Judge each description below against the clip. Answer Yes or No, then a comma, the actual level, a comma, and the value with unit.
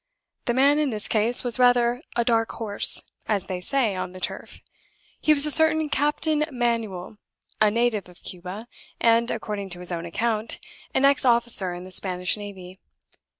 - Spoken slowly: No, average, 175 wpm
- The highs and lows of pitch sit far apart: No, average, 4.7 semitones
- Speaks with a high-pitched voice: Yes, high, 225 Hz